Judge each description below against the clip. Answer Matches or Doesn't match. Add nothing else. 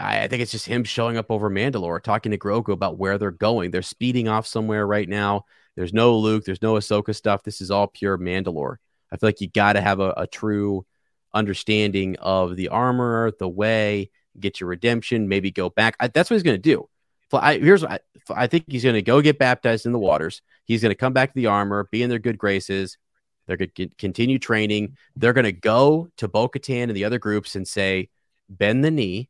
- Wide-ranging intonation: Doesn't match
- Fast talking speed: Matches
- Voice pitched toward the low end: Matches